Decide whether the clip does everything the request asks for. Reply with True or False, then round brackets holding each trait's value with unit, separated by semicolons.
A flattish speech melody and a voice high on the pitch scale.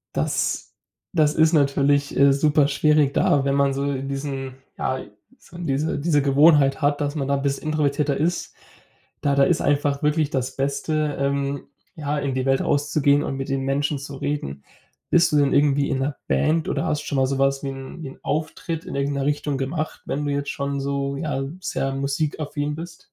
False (1.4 semitones; 140 Hz)